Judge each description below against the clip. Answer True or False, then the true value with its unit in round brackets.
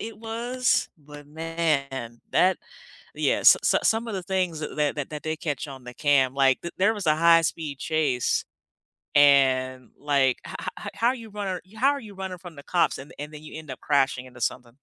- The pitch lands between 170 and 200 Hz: False (155 Hz)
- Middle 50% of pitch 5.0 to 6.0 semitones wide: True (5.3 semitones)